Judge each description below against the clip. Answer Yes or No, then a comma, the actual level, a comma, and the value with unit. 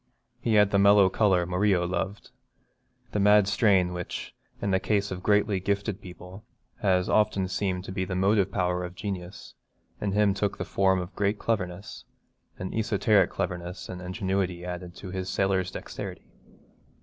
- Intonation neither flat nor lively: No, narrow, 2.0 semitones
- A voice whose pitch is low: Yes, very low, 95 Hz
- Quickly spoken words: No, average, 165 wpm